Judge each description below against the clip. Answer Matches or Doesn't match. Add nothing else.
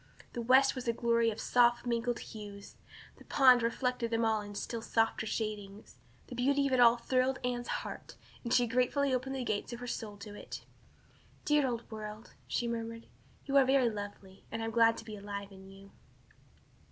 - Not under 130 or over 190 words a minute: Doesn't match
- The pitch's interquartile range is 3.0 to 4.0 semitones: Doesn't match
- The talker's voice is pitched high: Matches